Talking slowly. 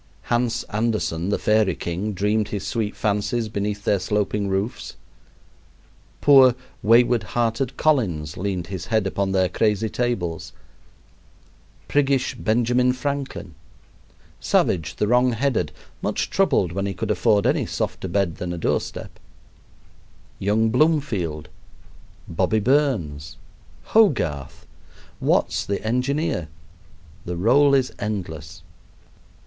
Yes: slow, 110 wpm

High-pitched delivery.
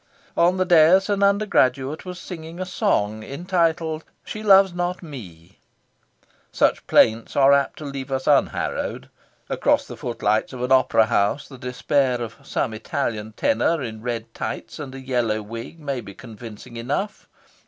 No: low, 135 Hz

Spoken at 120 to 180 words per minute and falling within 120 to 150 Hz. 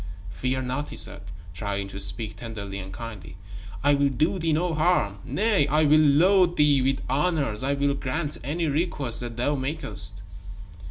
Yes: average, 170 wpm; medium, 140 Hz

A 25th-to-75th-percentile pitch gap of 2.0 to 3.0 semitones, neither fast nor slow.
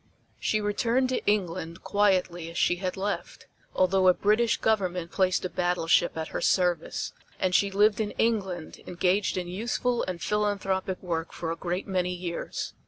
Yes: average, 2.7 semitones; average, 165 wpm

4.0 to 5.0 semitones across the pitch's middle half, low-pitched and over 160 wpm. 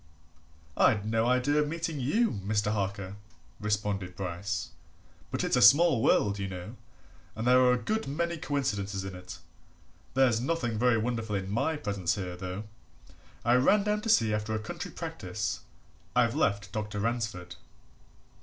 No: average, 4.4 semitones; low, 110 Hz; average, 155 wpm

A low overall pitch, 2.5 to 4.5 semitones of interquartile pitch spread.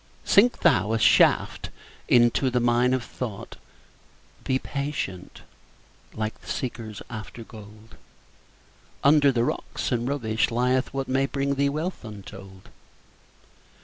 Yes: low, 120 Hz; average, 3.8 semitones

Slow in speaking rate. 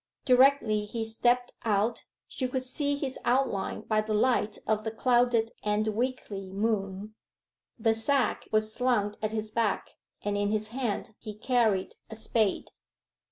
No: average, 150 wpm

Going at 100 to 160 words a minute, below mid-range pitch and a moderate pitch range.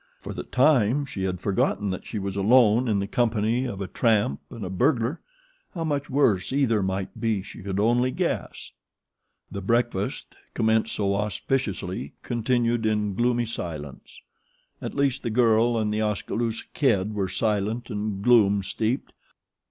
Yes: average, 155 wpm; low, 110 Hz; average, 3.4 semitones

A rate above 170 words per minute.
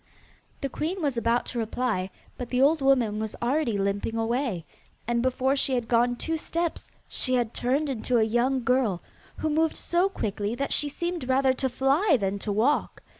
Yes: average, 185 wpm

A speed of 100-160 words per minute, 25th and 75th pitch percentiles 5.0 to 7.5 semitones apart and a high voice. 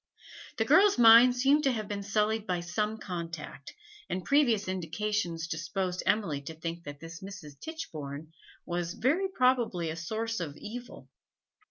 Yes: average, 150 wpm; average, 5.3 semitones; high, 195 Hz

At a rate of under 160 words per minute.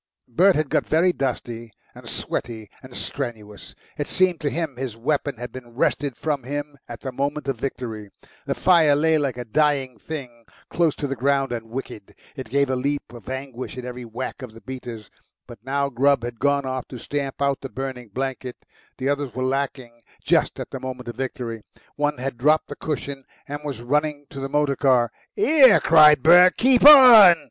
No: average, 195 wpm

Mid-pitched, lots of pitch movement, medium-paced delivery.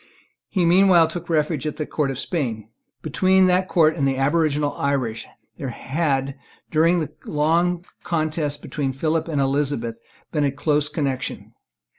No: medium, 150 Hz; average, 3.4 semitones; average, 150 wpm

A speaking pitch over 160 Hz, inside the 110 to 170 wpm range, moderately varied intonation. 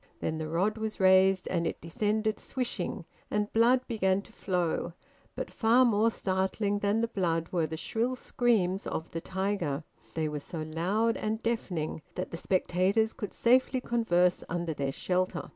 Yes: high, 190 Hz; average, 165 wpm; average, 4.5 semitones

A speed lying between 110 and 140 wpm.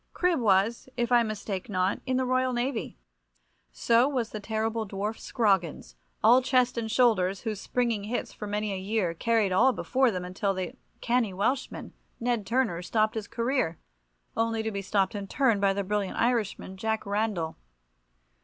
No: average, 170 wpm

